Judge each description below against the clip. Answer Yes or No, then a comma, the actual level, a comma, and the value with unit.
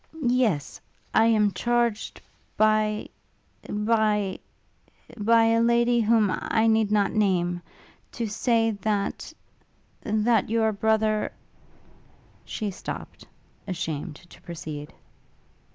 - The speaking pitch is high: Yes, high, 215 Hz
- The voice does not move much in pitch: Yes, narrow, 2.1 semitones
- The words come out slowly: Yes, slow, 100 wpm